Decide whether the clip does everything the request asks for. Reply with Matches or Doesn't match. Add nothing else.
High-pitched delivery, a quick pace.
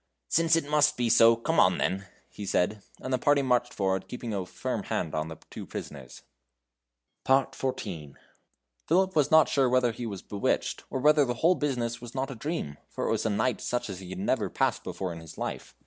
Doesn't match